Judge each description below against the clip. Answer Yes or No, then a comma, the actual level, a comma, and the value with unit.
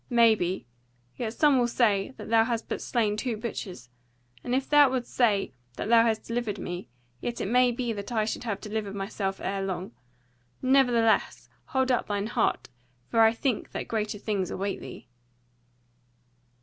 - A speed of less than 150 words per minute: No, average, 170 wpm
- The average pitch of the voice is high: Yes, high, 225 Hz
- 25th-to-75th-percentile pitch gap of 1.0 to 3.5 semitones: Yes, average, 3.1 semitones